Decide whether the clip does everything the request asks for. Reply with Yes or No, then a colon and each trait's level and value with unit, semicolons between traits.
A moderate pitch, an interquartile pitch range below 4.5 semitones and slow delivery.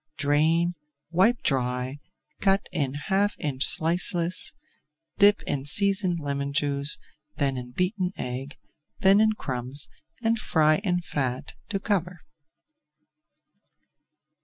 No: medium, 160 Hz; wide, 5.5 semitones; slow, 110 wpm